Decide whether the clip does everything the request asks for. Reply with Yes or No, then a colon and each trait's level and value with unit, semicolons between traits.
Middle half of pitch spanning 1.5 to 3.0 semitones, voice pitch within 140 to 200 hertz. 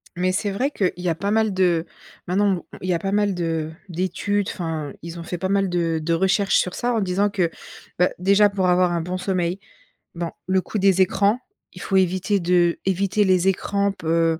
Yes: narrow, 2.4 semitones; medium, 185 Hz